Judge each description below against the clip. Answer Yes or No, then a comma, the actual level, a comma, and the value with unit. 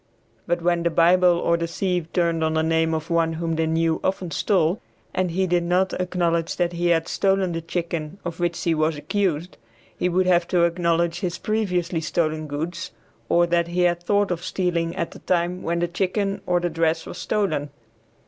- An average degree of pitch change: No, narrow, 1.5 semitones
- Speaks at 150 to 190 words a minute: No, average, 200 wpm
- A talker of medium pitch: Yes, medium, 170 Hz